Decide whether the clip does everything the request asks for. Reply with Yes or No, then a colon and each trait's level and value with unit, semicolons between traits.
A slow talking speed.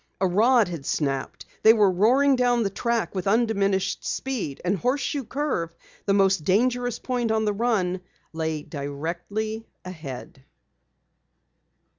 Yes: slow, 130 wpm